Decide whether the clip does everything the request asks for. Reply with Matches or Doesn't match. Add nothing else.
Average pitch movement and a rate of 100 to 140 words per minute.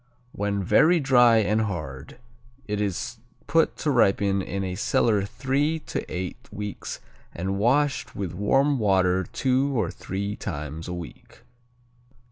Matches